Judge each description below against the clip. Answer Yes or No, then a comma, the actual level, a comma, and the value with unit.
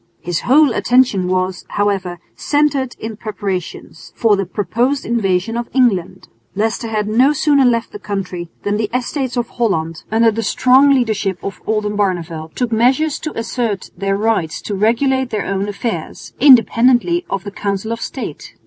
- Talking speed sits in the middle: Yes, average, 160 wpm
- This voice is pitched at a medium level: No, high, 220 Hz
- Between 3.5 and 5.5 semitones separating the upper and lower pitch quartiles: Yes, average, 4.1 semitones